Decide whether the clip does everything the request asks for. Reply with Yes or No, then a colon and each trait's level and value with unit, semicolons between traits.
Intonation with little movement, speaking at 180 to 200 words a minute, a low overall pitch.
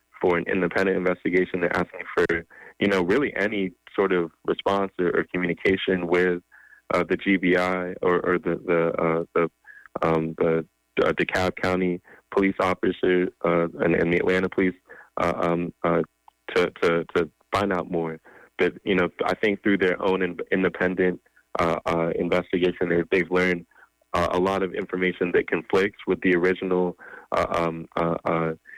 No: narrow, 1.5 semitones; average, 165 wpm; very low, 90 Hz